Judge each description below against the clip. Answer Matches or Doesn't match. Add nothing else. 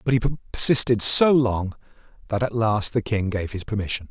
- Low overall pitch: Matches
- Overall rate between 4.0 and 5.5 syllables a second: Matches